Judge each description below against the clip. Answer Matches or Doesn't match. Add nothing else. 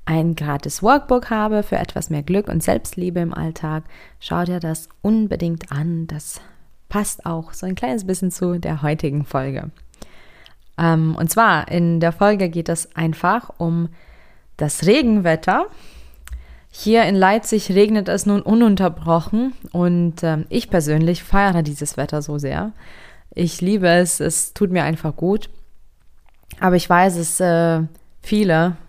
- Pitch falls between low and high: Matches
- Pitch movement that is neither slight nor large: Matches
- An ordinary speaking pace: Matches